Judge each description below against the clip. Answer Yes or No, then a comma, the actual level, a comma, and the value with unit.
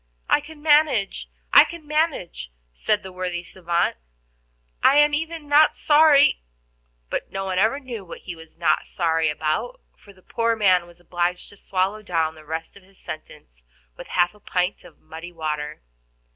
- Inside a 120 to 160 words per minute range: No, average, 175 wpm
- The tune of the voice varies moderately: No, wide, 8.0 semitones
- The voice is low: No, medium, 185 Hz